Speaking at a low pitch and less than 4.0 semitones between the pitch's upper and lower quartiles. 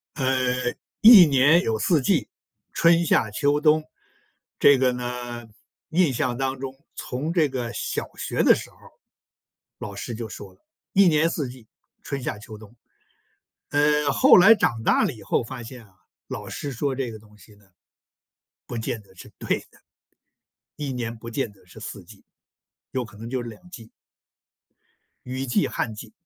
No: low, 125 Hz; average, 4.5 semitones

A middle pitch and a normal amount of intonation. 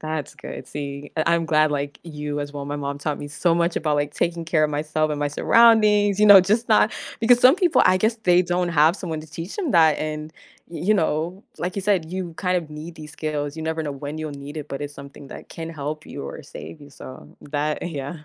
Yes: medium, 155 Hz; average, 3.4 semitones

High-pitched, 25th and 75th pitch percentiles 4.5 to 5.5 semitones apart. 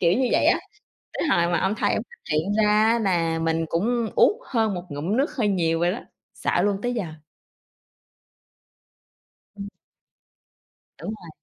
Yes: high, 200 Hz; average, 5.0 semitones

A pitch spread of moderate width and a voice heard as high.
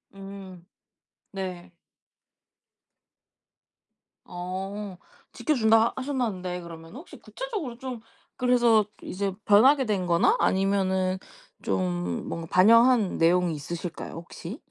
Yes: average, 4.6 semitones; high, 195 Hz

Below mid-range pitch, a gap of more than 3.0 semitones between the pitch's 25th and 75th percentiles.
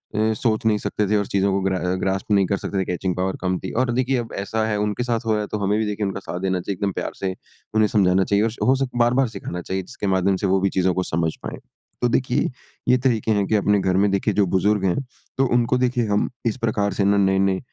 No: low, 100 Hz; average, 2.7 semitones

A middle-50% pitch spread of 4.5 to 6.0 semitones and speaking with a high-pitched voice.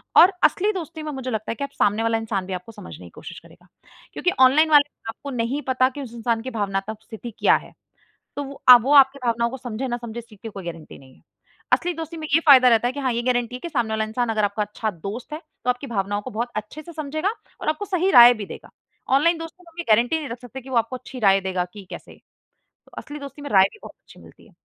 Yes: average, 4.8 semitones; high, 245 Hz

